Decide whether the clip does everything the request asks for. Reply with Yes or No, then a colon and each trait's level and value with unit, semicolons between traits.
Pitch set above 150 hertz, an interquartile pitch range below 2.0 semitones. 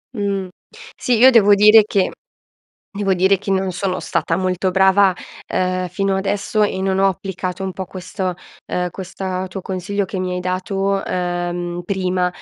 Yes: high, 190 Hz; narrow, 1.4 semitones